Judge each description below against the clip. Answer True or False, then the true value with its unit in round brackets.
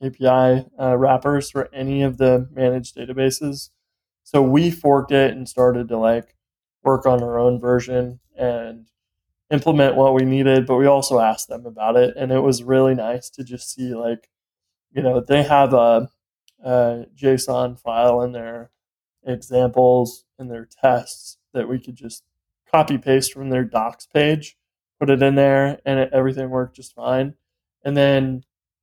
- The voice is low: True (130 Hz)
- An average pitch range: False (2.1 semitones)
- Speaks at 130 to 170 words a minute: True (165 wpm)